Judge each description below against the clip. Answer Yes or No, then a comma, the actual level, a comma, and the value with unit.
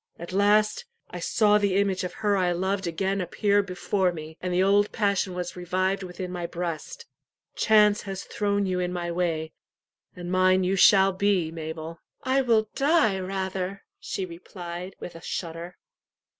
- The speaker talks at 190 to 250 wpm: No, average, 165 wpm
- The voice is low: No, medium, 185 Hz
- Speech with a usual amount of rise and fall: No, narrow, 2.3 semitones